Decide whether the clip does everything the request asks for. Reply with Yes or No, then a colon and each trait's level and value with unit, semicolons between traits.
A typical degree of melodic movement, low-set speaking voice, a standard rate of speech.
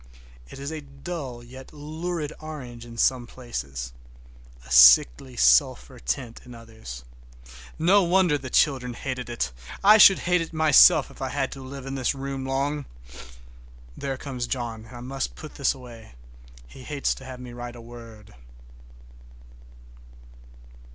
Yes: average, 3.5 semitones; low, 130 Hz; average, 150 wpm